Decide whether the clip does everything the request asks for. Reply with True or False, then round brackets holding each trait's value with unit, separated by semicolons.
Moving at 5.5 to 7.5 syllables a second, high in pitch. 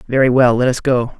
False (5.8 syllables/s; 125 Hz)